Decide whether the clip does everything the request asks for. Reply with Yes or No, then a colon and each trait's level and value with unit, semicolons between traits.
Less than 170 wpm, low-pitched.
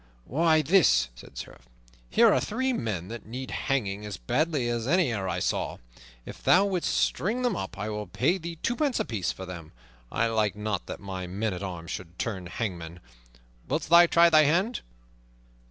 No: average, 185 wpm; low, 115 Hz